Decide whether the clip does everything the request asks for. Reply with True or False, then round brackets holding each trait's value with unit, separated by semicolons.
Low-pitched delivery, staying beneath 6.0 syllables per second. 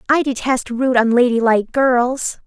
False (245 Hz; 4.5 syllables/s)